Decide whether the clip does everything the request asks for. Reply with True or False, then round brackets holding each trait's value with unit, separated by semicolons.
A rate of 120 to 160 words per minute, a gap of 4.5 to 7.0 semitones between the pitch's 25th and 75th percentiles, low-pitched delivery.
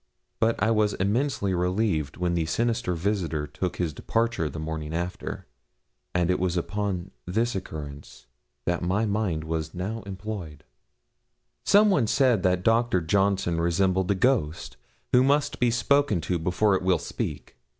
True (150 wpm; 4.8 semitones; 95 Hz)